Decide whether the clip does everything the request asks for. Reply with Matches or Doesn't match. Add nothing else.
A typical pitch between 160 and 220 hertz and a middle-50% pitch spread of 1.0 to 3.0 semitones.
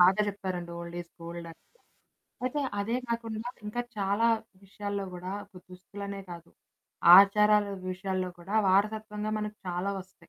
Matches